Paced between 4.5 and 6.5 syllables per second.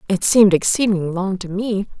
Yes: 5.8 syllables/s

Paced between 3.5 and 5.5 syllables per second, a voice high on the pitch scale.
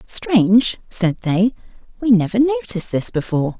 Yes: 4.8 syllables/s; high, 215 Hz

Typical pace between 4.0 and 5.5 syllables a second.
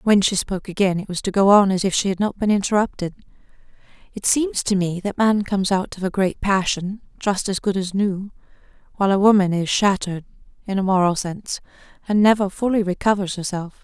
No: 5.9 syllables/s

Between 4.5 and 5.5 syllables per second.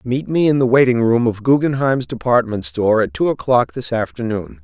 Yes: 5.3 syllables/s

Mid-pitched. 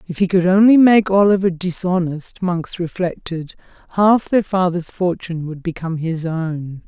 Yes: medium, 175 Hz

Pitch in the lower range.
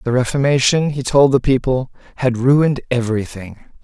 Yes: low, 130 Hz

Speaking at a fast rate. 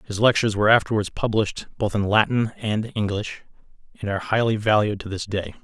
No: average, 180 wpm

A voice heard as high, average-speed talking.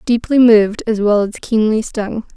Yes: high, 220 Hz; average, 180 wpm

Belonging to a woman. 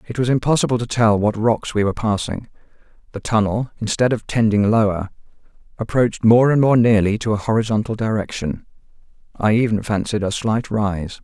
No: male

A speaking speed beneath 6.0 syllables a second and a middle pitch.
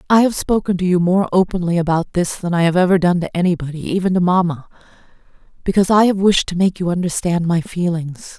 No: 6.1 syllables/s; medium, 180 Hz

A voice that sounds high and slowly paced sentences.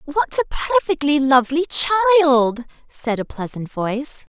Yes: very high, 285 Hz; slow, 125 wpm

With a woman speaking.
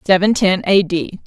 Yes: female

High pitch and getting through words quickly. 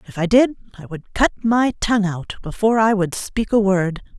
Yes: high, 205 Hz; fast, 215 wpm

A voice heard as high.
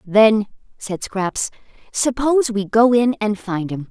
Yes: high, 215 Hz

